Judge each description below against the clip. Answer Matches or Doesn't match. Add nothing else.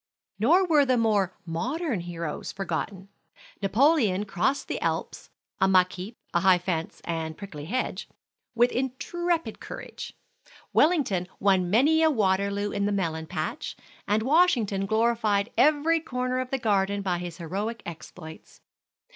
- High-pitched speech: Matches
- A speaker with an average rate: Doesn't match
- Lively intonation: Matches